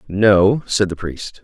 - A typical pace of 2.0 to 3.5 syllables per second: Yes, 3.2 syllables/s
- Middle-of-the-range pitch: No, low, 100 Hz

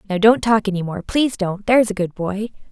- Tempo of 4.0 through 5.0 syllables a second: No, 6.1 syllables/s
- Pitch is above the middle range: Yes, high, 205 Hz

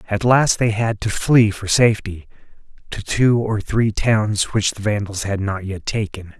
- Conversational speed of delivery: Yes, average, 190 wpm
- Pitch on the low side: Yes, low, 105 Hz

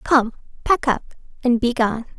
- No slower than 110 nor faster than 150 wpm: Yes, slow, 135 wpm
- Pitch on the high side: Yes, high, 245 Hz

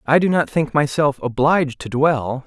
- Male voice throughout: Yes, male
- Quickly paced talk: No, average, 195 wpm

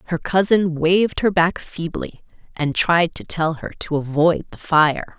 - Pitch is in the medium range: Yes, medium, 170 Hz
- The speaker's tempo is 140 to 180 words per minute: Yes, average, 175 wpm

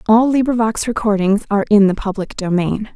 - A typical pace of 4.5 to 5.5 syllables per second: No, 5.7 syllables/s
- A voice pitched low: No, high, 210 Hz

